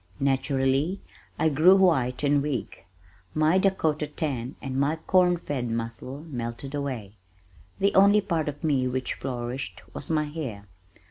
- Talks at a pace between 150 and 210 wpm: No, average, 140 wpm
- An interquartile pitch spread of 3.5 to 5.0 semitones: Yes, average, 3.9 semitones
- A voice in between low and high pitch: Yes, medium, 145 Hz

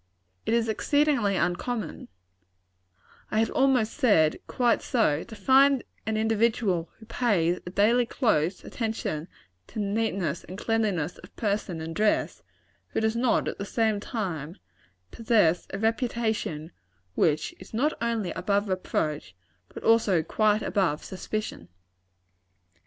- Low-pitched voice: No, high, 215 Hz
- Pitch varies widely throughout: No, average, 4.4 semitones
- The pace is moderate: No, slow, 130 wpm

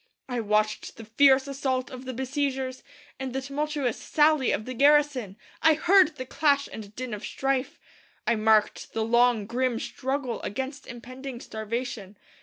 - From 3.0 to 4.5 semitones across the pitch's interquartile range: Yes, average, 3.4 semitones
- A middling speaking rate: Yes, average, 155 wpm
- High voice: Yes, very high, 255 Hz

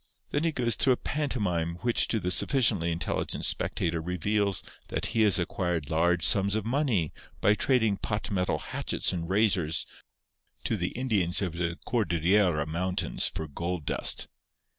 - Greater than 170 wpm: No, average, 155 wpm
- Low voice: Yes, very low, 95 Hz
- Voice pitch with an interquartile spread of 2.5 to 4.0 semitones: No, average, 4.5 semitones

